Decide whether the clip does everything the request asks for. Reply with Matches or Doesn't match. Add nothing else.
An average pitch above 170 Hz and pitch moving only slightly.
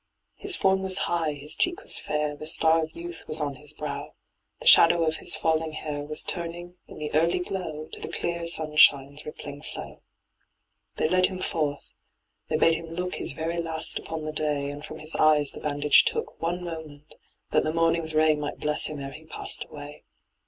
Doesn't match